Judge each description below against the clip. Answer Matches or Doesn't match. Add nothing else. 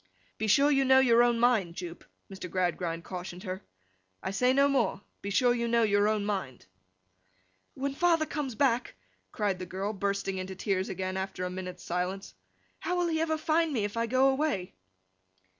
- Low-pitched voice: Doesn't match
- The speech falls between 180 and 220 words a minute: Matches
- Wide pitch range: Matches